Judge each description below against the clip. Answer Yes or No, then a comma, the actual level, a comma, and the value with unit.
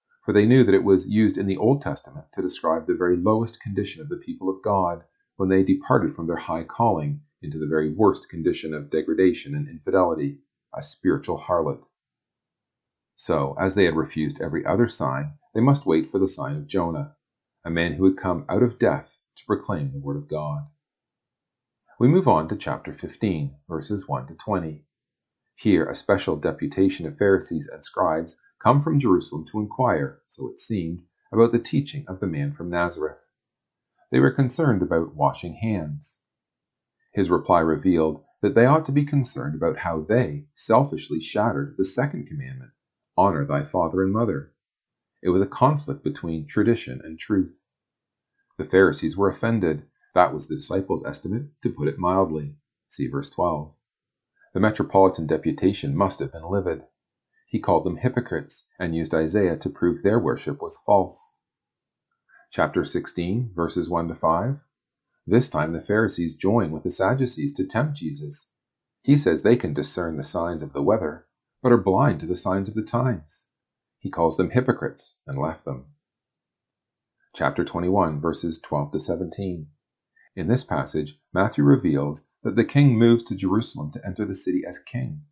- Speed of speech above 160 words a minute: Yes, average, 170 wpm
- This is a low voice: Yes, very low, 95 Hz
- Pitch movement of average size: No, wide, 7.0 semitones